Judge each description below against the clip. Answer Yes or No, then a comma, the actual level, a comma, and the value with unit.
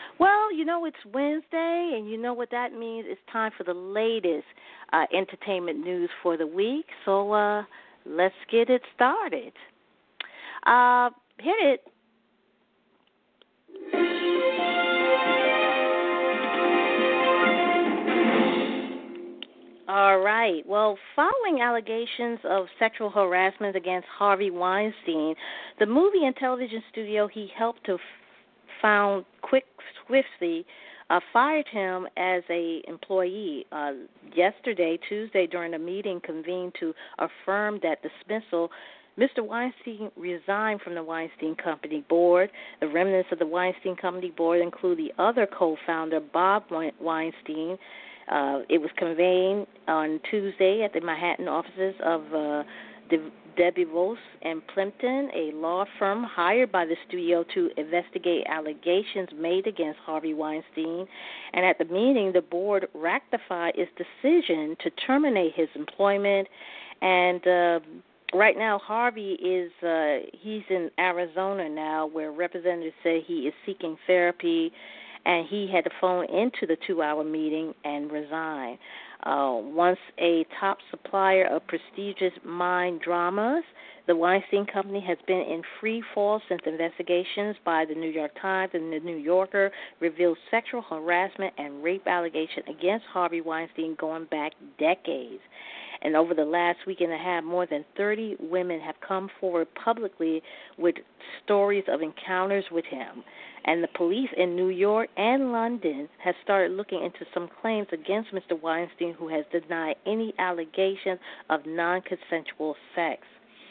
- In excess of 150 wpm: No, slow, 135 wpm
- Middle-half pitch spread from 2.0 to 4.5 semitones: Yes, average, 4.1 semitones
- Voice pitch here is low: No, medium, 185 Hz